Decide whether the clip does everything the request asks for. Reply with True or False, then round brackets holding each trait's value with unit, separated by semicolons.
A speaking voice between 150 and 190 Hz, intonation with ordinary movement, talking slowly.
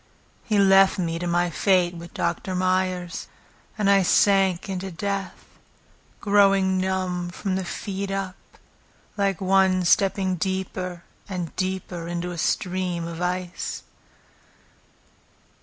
False (185 Hz; 1.6 semitones; 120 wpm)